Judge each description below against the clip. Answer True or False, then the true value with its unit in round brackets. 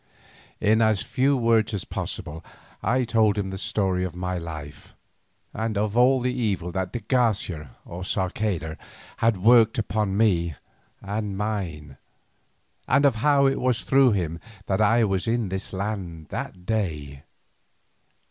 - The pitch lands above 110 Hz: False (105 Hz)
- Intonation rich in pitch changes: False (4.0 semitones)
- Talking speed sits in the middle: True (145 wpm)